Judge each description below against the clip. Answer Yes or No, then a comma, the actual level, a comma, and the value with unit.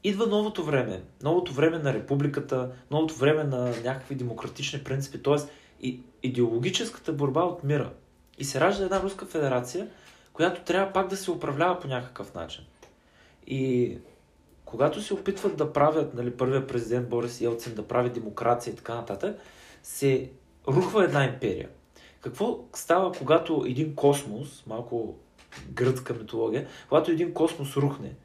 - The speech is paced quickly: No, average, 140 wpm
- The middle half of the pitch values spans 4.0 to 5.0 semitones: Yes, average, 4.7 semitones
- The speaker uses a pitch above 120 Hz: Yes, medium, 140 Hz